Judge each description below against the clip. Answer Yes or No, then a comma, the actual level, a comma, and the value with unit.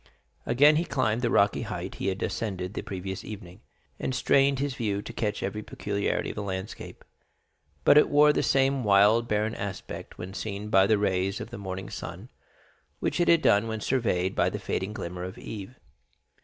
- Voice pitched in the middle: No, low, 105 Hz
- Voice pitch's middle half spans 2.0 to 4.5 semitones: Yes, average, 4.0 semitones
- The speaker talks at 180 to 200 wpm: Yes, average, 190 wpm